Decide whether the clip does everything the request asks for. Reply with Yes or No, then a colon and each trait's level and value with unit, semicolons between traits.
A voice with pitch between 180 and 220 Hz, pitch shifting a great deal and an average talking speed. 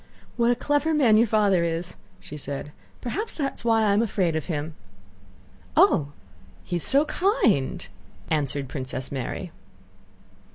Yes: high, 190 Hz; wide, 8.3 semitones; average, 150 wpm